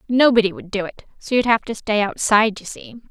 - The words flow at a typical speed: No, fast, 230 wpm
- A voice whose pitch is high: Yes, high, 220 Hz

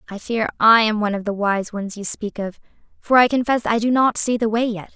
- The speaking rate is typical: No, fast, 265 wpm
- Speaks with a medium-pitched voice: No, high, 220 Hz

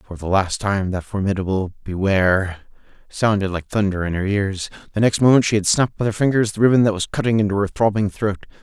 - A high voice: No, low, 100 Hz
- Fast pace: Yes, fast, 215 wpm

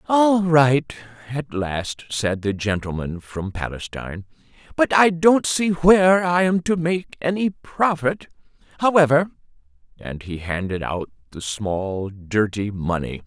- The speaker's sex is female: No, male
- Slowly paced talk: Yes, slow, 130 wpm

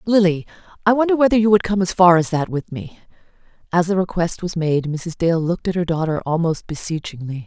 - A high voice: No, medium, 175 Hz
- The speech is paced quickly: Yes, fast, 210 wpm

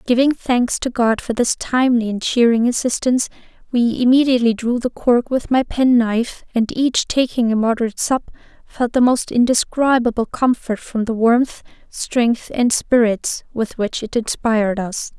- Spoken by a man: No, female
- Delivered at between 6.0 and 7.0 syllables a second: No, 4.7 syllables/s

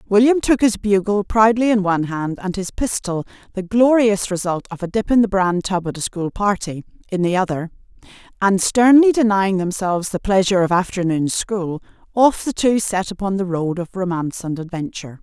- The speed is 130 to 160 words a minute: No, average, 190 wpm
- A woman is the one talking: Yes, female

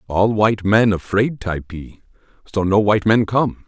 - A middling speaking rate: Yes, average, 165 wpm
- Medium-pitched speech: No, low, 100 Hz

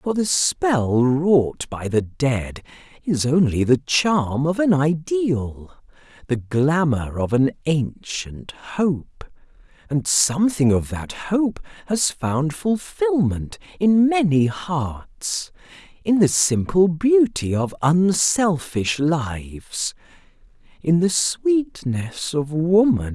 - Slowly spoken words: Yes, slow, 105 wpm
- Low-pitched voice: No, medium, 155 Hz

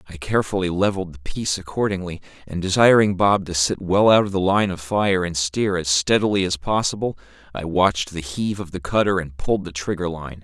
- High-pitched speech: No, very low, 95 Hz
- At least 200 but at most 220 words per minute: Yes, fast, 205 wpm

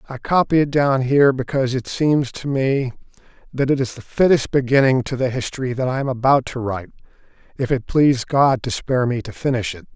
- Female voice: No, male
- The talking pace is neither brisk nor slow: No, fast, 210 wpm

